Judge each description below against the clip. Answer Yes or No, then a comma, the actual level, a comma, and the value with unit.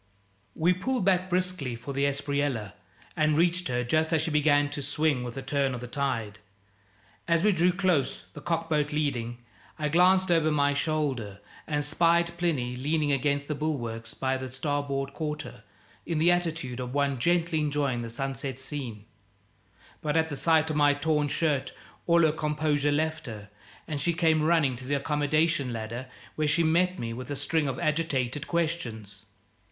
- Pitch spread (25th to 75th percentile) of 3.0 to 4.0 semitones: Yes, average, 3.5 semitones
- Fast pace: No, average, 175 wpm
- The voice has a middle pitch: Yes, medium, 145 Hz